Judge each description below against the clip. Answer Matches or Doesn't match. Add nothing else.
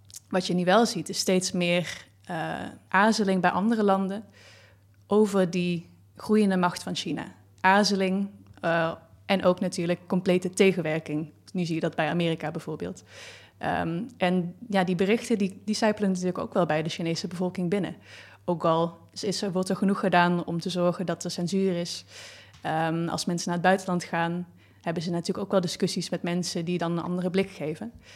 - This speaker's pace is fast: Doesn't match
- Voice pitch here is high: Doesn't match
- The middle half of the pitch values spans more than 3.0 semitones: Doesn't match